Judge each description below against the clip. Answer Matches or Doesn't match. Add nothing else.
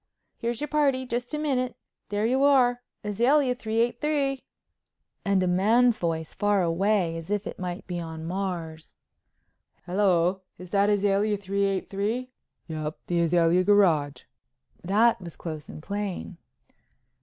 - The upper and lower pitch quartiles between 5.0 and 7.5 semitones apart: Matches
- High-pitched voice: Matches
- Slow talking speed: Matches